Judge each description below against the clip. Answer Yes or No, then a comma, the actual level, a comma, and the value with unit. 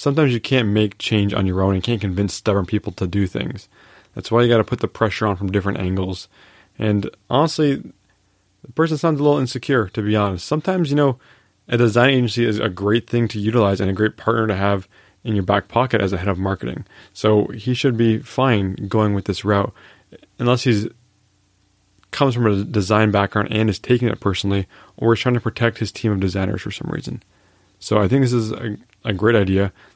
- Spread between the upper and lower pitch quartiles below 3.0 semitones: No, average, 3.3 semitones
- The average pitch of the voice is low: Yes, low, 105 Hz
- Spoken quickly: Yes, fast, 220 wpm